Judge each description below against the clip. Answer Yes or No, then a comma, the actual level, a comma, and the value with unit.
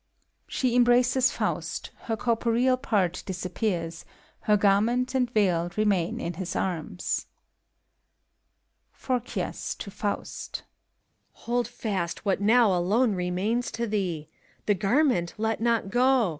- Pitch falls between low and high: No, high, 215 Hz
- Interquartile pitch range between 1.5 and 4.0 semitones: No, average, 4.7 semitones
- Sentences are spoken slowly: Yes, slow, 120 wpm